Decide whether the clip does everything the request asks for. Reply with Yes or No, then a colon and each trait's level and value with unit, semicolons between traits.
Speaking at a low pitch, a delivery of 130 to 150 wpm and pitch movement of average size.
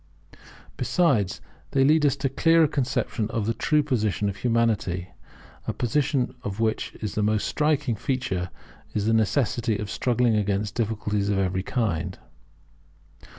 Yes: low, 115 Hz; average, 145 wpm; average, 4.6 semitones